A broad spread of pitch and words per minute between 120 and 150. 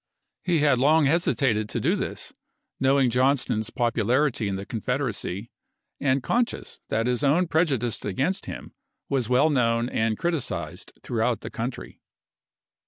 No: average, 4.3 semitones; average, 145 wpm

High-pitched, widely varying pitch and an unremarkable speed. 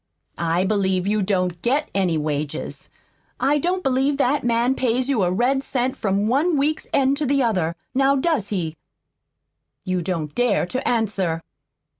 Yes: high, 230 Hz; wide, 6.7 semitones; average, 160 wpm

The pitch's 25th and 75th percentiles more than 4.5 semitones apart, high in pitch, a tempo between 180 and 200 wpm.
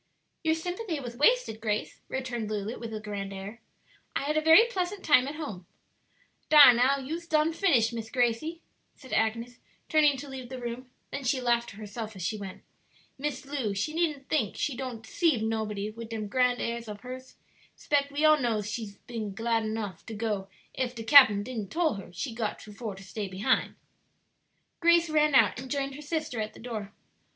Yes: average, 5.1 semitones; high, 245 Hz; average, 195 wpm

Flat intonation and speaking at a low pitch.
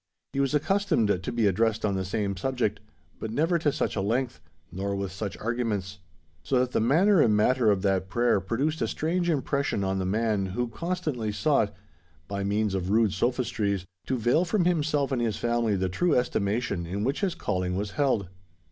No: wide, 5.5 semitones; low, 115 Hz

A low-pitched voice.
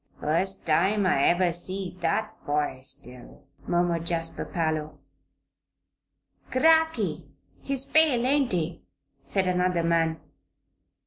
No: medium, 175 Hz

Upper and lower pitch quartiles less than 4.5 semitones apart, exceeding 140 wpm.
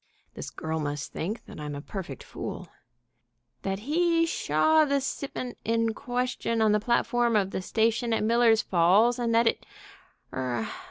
No: average, 5.2 semitones; average, 160 wpm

